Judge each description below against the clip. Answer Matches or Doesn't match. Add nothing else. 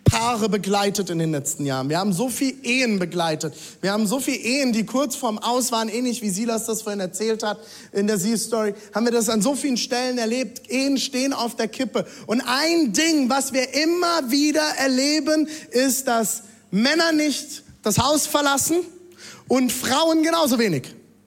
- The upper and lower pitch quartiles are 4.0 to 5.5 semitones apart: Matches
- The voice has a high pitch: Matches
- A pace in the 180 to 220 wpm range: Matches